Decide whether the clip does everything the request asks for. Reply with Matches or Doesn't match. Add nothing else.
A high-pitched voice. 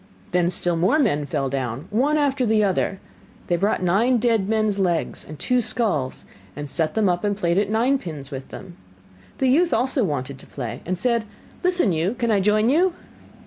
Matches